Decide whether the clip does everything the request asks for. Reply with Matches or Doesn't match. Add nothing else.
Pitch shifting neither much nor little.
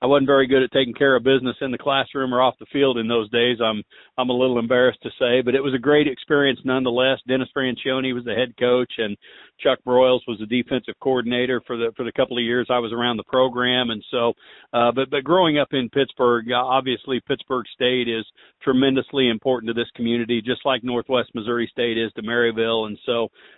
Doesn't match